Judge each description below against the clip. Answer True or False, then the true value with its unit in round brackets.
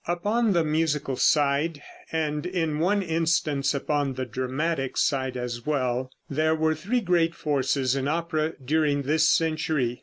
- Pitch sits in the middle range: True (155 Hz)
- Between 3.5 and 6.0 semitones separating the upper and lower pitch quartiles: False (3.1 semitones)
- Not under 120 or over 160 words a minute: True (145 wpm)